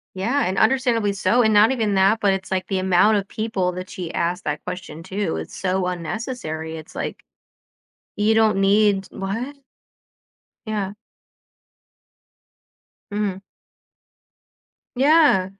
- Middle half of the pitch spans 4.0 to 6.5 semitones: No, average, 3.0 semitones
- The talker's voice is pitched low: No, high, 195 Hz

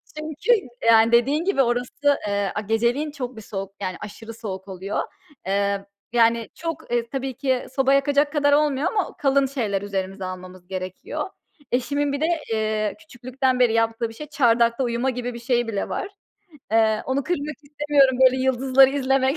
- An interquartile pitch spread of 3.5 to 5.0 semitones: Yes, average, 4.2 semitones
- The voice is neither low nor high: No, high, 245 Hz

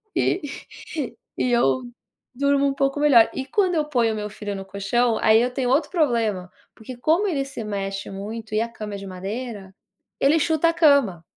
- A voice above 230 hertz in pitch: Yes, high, 240 Hz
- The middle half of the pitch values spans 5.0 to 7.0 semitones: Yes, average, 5.3 semitones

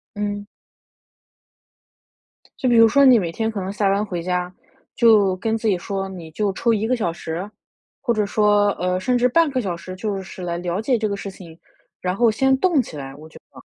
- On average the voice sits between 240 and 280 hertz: No, high, 205 Hz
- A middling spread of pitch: Yes, average, 3.8 semitones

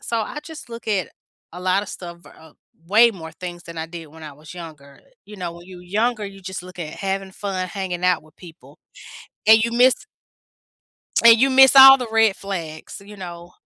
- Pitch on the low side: No, medium, 185 Hz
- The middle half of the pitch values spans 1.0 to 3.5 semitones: No, average, 4.3 semitones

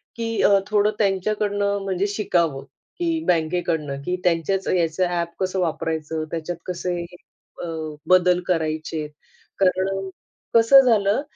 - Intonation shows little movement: No, average, 3.4 semitones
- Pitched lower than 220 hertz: Yes, medium, 185 Hz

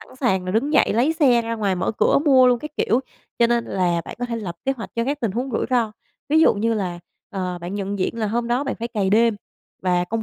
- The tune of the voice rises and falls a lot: No, average, 4.0 semitones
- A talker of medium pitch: No, high, 230 Hz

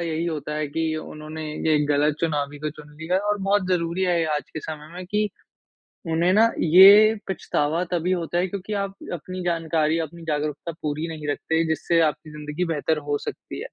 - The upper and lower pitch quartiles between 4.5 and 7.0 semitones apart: No, average, 2.9 semitones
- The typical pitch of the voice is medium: Yes, medium, 165 Hz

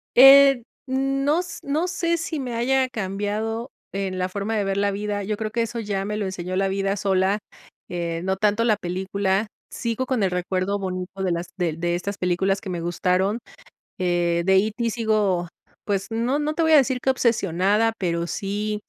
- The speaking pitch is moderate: No, high, 205 Hz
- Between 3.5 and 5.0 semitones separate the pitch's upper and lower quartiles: Yes, average, 4.0 semitones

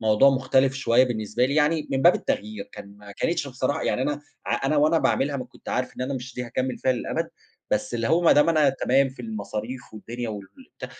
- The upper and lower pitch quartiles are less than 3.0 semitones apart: No, average, 3.3 semitones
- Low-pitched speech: Yes, low, 130 Hz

